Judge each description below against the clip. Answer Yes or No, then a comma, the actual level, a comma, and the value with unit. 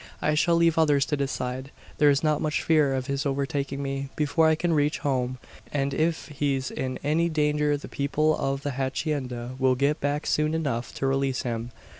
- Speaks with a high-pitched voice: No, medium, 140 Hz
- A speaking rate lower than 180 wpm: No, average, 190 wpm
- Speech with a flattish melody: Yes, narrow, 2.1 semitones